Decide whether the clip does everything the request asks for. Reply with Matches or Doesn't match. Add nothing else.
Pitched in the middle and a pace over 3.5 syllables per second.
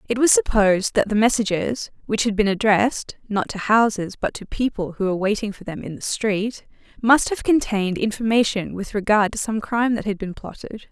Doesn't match